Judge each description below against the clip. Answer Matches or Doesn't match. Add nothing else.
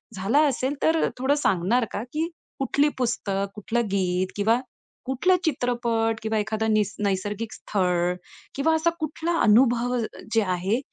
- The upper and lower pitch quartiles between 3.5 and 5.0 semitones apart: Matches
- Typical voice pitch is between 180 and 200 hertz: Doesn't match